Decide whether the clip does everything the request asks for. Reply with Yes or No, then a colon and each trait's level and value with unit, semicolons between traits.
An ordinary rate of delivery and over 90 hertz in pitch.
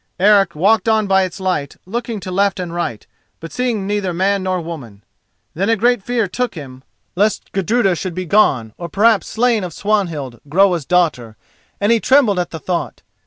Yes: average, 185 wpm; high, 190 Hz